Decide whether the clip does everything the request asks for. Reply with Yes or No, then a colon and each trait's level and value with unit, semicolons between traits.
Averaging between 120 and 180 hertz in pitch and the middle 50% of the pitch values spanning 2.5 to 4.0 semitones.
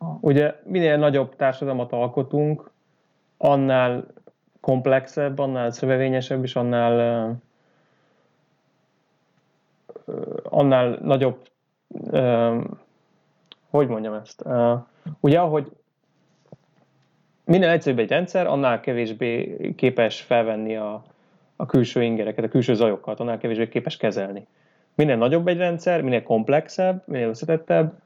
No: low, 130 Hz; average, 4.8 semitones